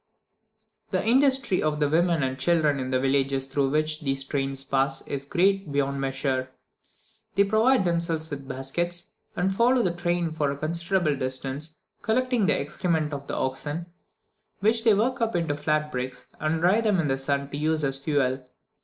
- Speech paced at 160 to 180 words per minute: Yes, average, 175 wpm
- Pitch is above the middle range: No, medium, 155 Hz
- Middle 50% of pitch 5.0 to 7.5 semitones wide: No, average, 4.6 semitones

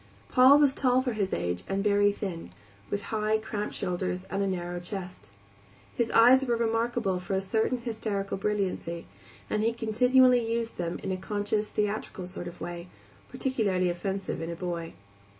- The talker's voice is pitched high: Yes, high, 205 Hz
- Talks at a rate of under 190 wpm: Yes, average, 170 wpm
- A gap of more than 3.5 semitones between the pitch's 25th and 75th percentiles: Yes, average, 3.9 semitones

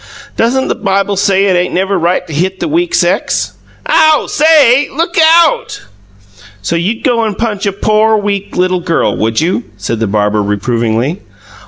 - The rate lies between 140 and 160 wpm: No, average, 170 wpm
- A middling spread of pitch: No, wide, 6.1 semitones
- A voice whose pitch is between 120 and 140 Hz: No, high, 195 Hz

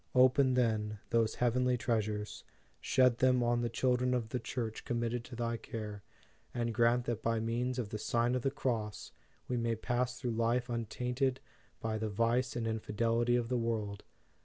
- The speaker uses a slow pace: No, average, 180 wpm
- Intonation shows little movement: Yes, narrow, 1.8 semitones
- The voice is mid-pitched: No, low, 120 Hz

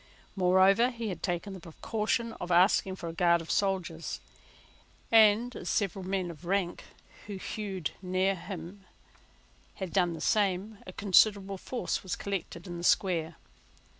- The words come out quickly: No, average, 150 wpm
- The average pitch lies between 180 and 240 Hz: Yes, high, 190 Hz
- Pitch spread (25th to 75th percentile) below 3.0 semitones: Yes, narrow, 2.6 semitones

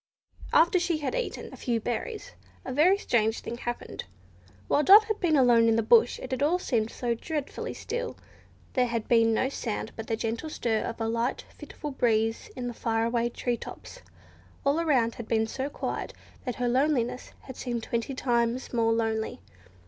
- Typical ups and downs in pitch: Yes, average, 4.0 semitones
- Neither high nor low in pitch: No, high, 240 Hz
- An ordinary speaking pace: Yes, average, 185 wpm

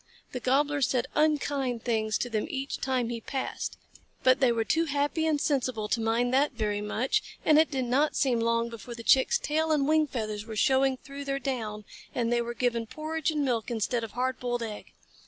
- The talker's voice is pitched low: No, very high, 255 Hz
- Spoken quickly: Yes, fast, 210 wpm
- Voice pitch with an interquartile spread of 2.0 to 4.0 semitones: Yes, average, 3.6 semitones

